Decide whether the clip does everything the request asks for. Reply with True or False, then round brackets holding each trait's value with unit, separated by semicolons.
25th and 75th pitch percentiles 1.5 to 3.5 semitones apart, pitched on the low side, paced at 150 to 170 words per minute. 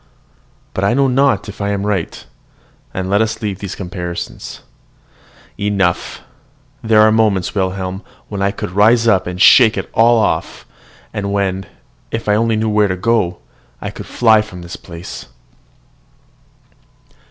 True (2.8 semitones; 100 Hz; 155 wpm)